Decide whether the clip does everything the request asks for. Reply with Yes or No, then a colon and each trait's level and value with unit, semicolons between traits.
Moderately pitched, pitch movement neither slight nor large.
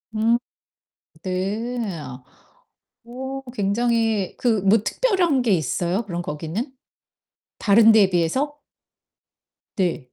No: high, 220 Hz; average, 4.6 semitones